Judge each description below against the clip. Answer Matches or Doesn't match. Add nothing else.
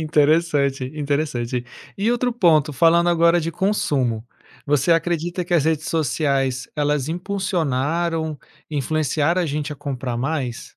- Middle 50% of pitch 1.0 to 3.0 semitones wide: Doesn't match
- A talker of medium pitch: Matches